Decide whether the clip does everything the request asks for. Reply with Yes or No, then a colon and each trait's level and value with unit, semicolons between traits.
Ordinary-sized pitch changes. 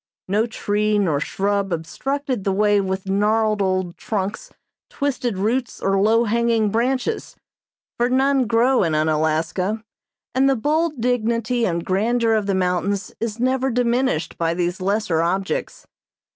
Yes: average, 4.2 semitones